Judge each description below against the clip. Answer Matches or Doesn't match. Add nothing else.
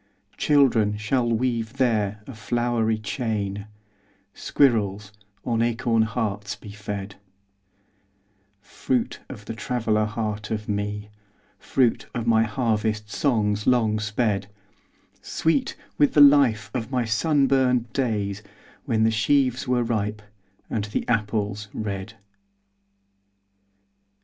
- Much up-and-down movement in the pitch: Doesn't match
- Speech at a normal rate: Doesn't match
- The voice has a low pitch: Matches